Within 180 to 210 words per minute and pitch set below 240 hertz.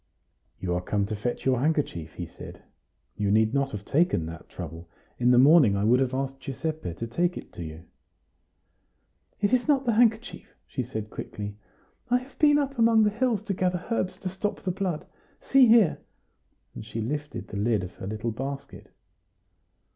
Yes: average, 185 wpm; low, 135 Hz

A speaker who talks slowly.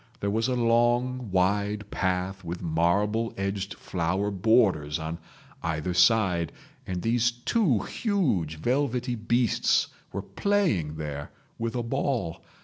Yes: slow, 125 wpm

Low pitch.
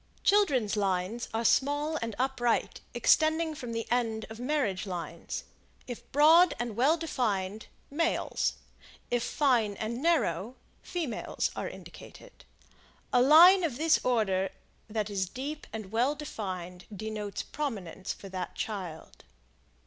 No: high, 235 Hz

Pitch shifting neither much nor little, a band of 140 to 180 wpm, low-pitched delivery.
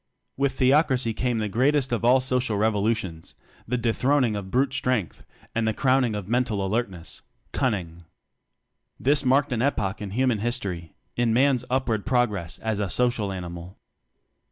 Yes: average, 4.0 semitones; average, 160 wpm; low, 115 Hz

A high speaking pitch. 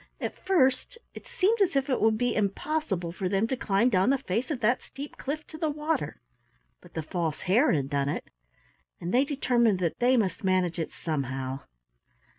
Yes: high, 225 Hz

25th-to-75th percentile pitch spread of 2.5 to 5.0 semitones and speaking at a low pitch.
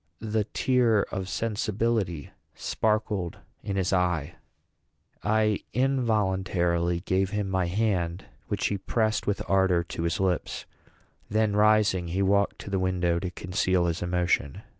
Yes: average, 3.4 semitones; very low, 95 Hz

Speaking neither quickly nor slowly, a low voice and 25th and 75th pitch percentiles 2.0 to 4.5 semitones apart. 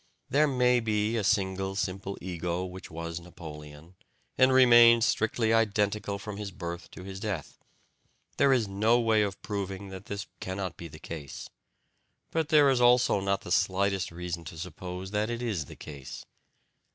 Yes: average, 165 wpm; low, 100 Hz; average, 4.0 semitones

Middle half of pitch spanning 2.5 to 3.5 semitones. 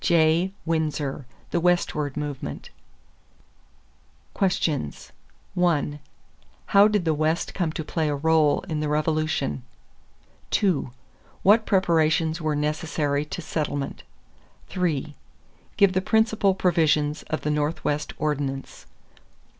Yes: average, 3.0 semitones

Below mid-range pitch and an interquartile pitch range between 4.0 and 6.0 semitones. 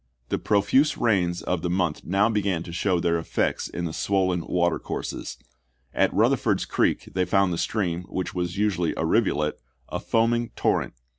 No: very low, 90 Hz; average, 2.9 semitones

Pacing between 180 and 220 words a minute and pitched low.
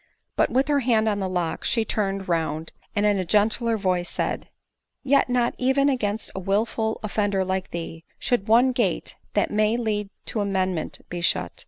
No: average, 185 wpm; high, 205 Hz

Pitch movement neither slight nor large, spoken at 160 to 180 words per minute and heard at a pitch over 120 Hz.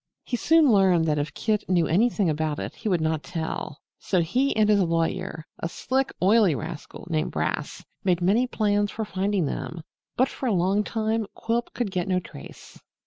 No: average, 4.8 semitones; average, 190 wpm; high, 190 Hz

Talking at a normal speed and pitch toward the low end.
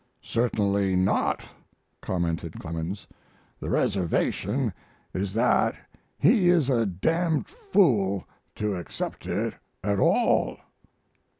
No: slow, 100 wpm; low, 100 Hz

